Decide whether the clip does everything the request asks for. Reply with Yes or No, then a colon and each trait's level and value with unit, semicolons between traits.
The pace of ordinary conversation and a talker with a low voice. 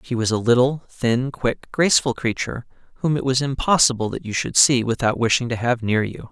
No: fast, 210 wpm; low, 125 Hz